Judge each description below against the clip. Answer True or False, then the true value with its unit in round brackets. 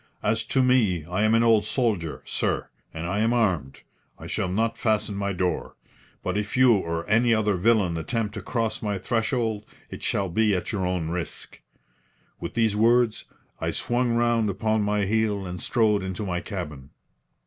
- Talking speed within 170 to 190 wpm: True (180 wpm)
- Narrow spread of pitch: False (3.7 semitones)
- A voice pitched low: True (105 Hz)